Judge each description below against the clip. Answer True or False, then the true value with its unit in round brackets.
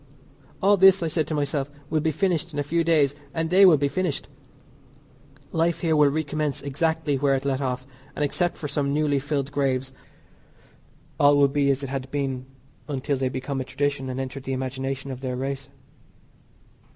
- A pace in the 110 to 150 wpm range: False (190 wpm)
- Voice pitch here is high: False (140 Hz)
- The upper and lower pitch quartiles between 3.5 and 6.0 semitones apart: False (2.7 semitones)